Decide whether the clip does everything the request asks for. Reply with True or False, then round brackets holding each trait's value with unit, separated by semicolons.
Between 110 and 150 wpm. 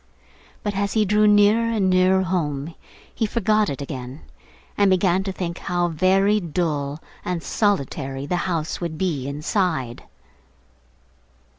True (135 wpm)